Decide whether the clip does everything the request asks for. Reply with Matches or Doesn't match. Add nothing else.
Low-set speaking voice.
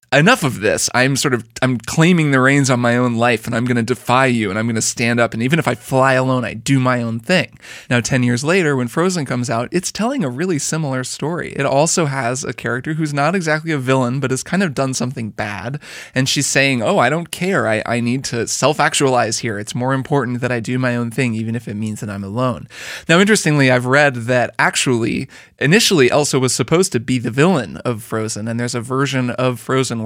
Matches